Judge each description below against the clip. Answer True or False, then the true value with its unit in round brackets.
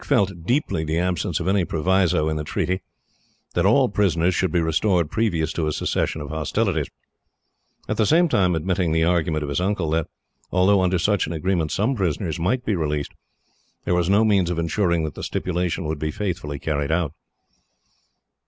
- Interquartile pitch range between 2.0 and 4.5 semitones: True (3.3 semitones)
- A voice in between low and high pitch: False (85 Hz)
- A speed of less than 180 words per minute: False (190 wpm)